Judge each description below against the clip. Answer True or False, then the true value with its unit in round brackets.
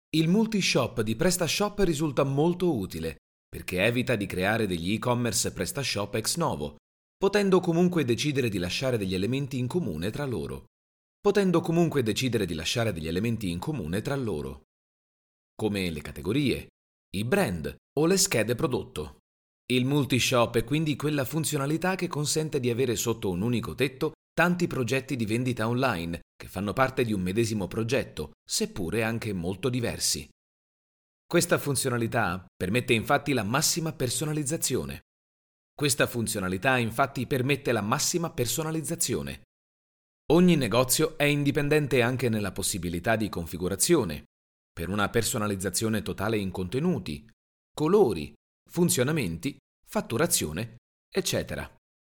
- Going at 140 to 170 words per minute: False (120 wpm)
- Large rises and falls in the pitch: True (7.8 semitones)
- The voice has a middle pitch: False (120 Hz)